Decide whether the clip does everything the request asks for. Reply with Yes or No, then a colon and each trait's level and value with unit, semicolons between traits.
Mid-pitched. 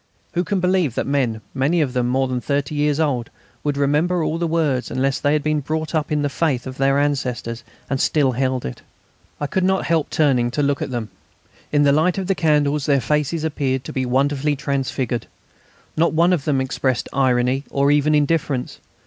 Yes: medium, 145 Hz